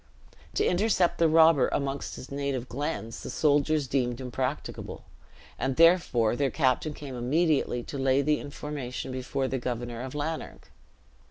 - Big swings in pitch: No, average, 3.0 semitones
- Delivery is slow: No, average, 145 wpm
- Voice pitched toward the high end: No, medium, 140 Hz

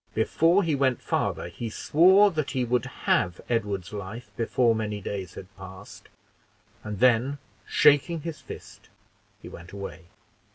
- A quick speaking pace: No, average, 140 wpm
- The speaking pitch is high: No, low, 115 Hz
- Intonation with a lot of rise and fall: Yes, wide, 6.5 semitones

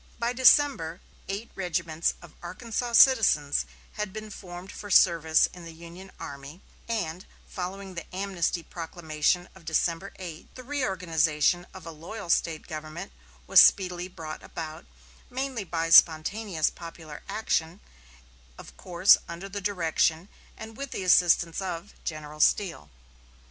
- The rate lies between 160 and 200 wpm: No, slow, 135 wpm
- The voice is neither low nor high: Yes, medium, 175 Hz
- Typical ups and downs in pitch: Yes, average, 3.5 semitones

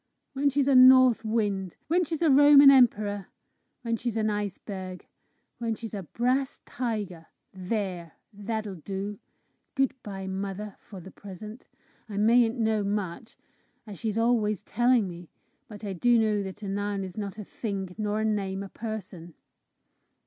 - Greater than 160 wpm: No, average, 155 wpm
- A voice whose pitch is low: No, high, 210 Hz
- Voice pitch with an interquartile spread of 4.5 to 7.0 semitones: No, average, 3.2 semitones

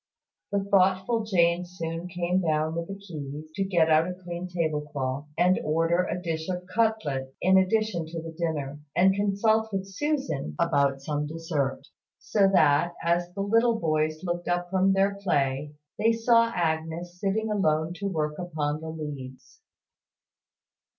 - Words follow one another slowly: No, average, 155 wpm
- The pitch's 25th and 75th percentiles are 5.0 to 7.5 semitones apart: No, average, 3.7 semitones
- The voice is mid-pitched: Yes, medium, 175 Hz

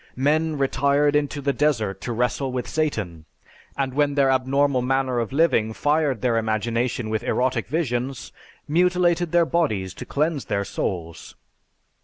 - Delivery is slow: No, average, 145 wpm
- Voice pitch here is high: No, low, 135 Hz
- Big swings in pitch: No, average, 4.2 semitones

